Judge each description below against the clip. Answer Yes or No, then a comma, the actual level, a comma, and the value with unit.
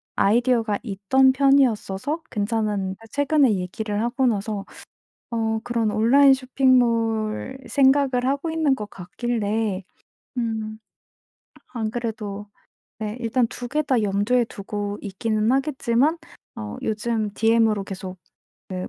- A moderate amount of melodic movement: Yes, average, 3.7 semitones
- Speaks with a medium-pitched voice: No, high, 225 Hz